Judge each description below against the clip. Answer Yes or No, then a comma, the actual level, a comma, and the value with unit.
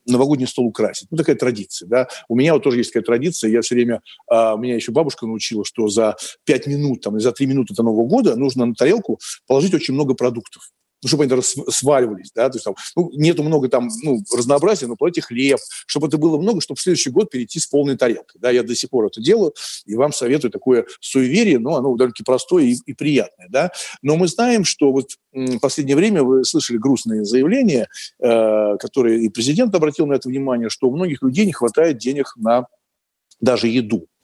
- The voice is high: No, low, 130 Hz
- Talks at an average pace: No, fast, 210 wpm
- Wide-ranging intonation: No, average, 3.7 semitones